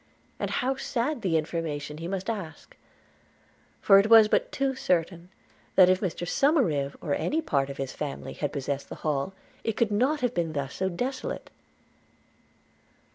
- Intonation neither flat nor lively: No, wide, 7.6 semitones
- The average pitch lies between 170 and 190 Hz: Yes, medium, 185 Hz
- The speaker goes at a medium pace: Yes, average, 160 wpm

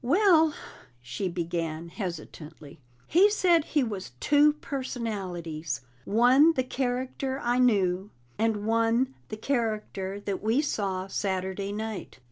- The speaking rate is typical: No, slow, 115 wpm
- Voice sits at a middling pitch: No, high, 220 Hz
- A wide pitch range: Yes, wide, 5.8 semitones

